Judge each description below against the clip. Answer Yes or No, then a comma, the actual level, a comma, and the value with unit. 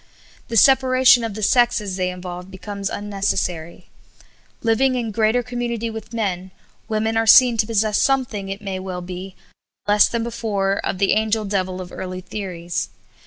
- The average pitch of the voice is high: Yes, high, 210 Hz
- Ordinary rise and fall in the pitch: Yes, average, 3.4 semitones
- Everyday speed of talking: Yes, average, 165 wpm